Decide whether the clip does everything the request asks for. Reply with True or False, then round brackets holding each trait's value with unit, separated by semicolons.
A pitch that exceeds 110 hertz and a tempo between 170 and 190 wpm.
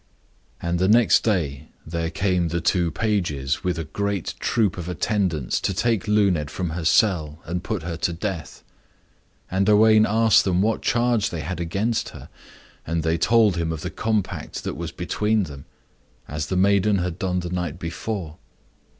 False (90 Hz; 175 wpm)